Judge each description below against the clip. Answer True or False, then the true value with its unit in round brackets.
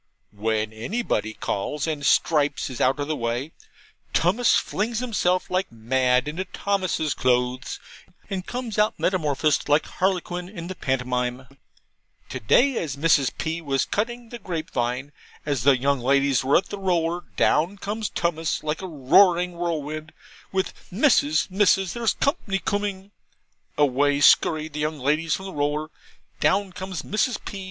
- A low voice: False (160 Hz)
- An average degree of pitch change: False (5.7 semitones)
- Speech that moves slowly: False (150 wpm)